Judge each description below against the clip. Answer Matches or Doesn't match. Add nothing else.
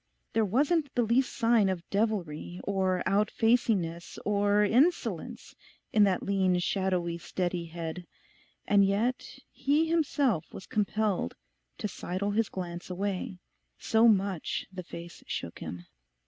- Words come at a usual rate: Doesn't match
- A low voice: Doesn't match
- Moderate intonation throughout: Matches